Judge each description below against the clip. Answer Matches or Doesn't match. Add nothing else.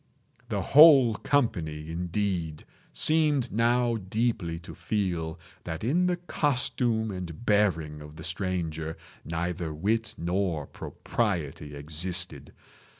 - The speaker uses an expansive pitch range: Matches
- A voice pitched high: Doesn't match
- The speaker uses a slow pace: Matches